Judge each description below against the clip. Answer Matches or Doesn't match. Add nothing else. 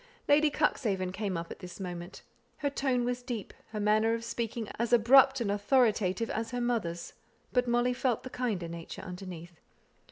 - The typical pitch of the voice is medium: Doesn't match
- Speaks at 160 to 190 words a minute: Matches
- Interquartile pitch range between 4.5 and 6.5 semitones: Matches